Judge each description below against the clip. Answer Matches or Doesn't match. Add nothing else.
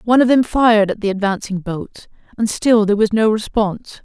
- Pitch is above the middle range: Matches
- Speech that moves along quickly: Matches